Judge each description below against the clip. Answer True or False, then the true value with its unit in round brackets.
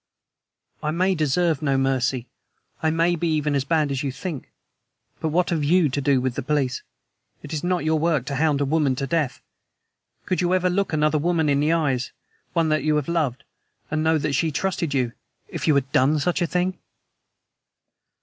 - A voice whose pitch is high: False (155 Hz)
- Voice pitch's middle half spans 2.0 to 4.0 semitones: True (3.3 semitones)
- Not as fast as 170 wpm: False (200 wpm)